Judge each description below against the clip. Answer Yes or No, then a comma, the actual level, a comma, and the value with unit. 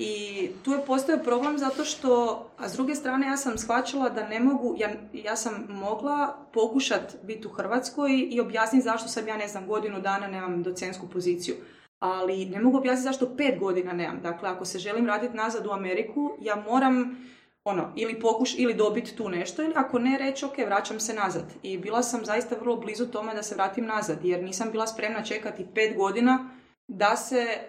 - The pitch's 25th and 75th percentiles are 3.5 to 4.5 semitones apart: Yes, average, 3.9 semitones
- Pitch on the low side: No, high, 225 Hz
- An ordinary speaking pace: No, fast, 195 wpm